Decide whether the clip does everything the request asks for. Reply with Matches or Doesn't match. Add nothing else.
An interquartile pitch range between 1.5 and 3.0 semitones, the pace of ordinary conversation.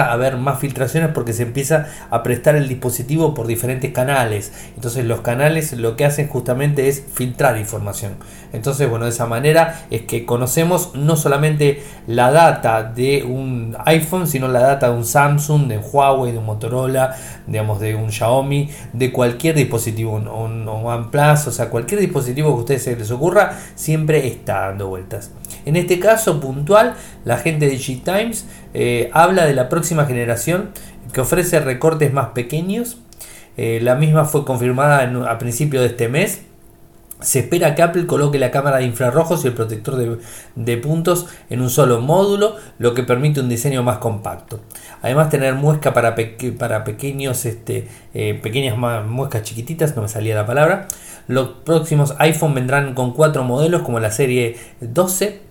Doesn't match